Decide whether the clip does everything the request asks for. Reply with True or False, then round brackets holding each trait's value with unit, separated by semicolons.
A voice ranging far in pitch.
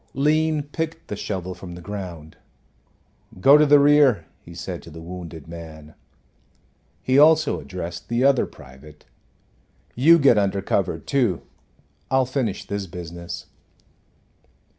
True (8.5 semitones)